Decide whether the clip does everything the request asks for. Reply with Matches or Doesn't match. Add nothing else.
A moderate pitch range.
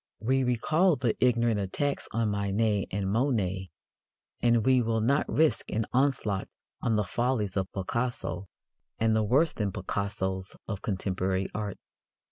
Matches